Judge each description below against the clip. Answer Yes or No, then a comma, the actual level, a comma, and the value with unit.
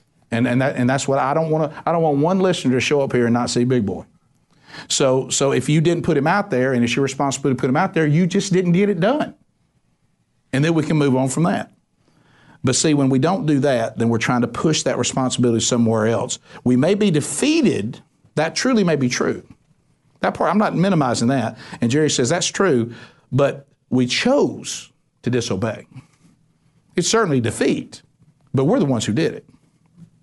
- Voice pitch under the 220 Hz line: Yes, medium, 140 Hz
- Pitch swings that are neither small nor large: Yes, average, 4.5 semitones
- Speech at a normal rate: No, fast, 210 wpm